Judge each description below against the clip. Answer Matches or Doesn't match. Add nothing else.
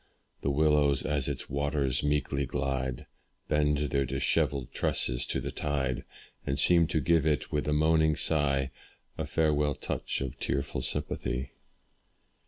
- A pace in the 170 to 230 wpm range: Doesn't match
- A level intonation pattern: Matches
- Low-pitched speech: Matches